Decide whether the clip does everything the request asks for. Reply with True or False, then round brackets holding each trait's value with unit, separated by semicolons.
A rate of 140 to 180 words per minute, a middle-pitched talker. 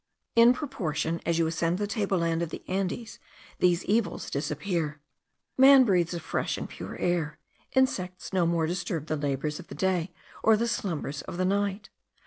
True (175 wpm; 180 Hz)